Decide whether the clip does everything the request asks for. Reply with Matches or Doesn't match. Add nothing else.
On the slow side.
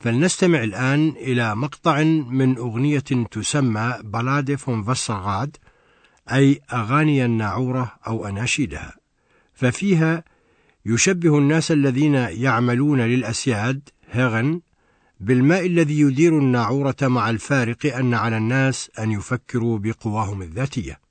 Doesn't match